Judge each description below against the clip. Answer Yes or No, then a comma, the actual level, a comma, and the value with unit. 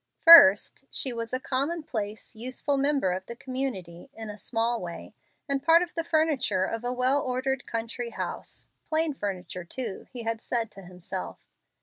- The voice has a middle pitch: No, high, 245 Hz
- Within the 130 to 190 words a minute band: Yes, average, 165 wpm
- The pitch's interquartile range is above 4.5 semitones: Yes, average, 4.9 semitones